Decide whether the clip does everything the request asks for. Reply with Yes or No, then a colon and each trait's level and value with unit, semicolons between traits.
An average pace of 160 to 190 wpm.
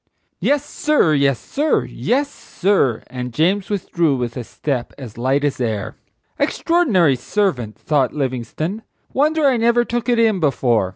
No: average, 150 wpm